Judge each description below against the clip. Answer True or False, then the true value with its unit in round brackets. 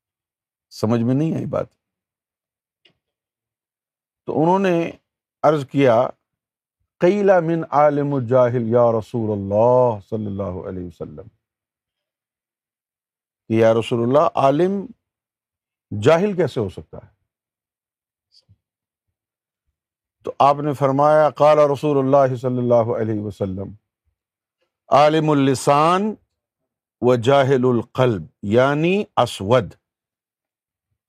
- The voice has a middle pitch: False (120 Hz)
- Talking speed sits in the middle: False (95 wpm)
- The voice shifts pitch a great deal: False (4.8 semitones)